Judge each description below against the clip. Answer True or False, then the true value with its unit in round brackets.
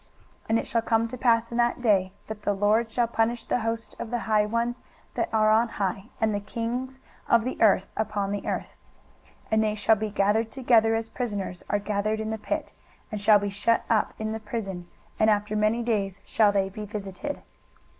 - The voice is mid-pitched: False (220 Hz)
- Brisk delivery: True (215 wpm)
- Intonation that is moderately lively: False (1.9 semitones)